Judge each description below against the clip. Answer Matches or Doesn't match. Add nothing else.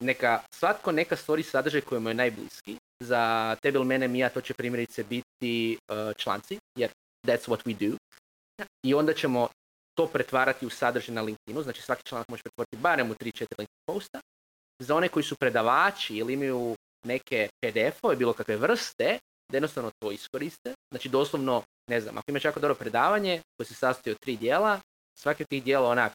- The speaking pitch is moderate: Doesn't match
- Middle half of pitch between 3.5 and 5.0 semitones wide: Matches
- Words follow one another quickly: Matches